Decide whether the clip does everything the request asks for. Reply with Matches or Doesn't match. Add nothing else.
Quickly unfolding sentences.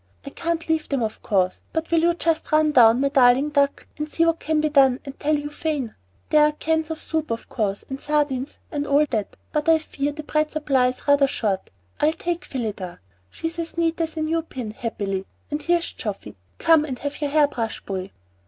Matches